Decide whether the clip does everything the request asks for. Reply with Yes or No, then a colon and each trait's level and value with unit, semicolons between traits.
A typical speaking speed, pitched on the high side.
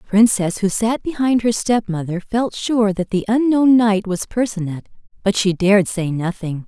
Yes: average, 180 wpm; high, 210 Hz